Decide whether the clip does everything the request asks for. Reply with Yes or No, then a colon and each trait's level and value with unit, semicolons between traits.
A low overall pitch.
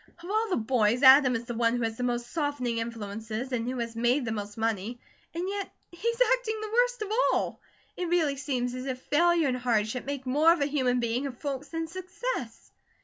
No: very high, 255 Hz